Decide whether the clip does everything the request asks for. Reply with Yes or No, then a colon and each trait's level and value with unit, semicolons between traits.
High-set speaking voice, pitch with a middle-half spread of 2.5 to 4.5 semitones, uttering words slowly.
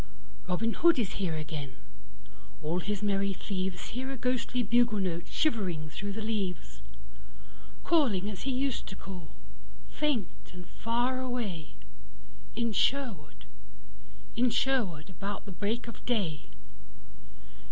No: high, 205 Hz; average, 5.3 semitones; slow, 115 wpm